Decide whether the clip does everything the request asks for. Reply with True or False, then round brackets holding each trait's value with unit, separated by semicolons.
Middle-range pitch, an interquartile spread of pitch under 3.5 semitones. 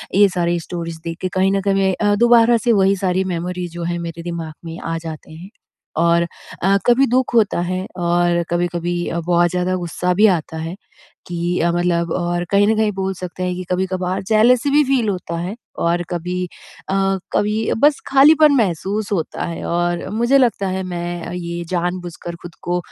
True (180 Hz; 2.8 semitones)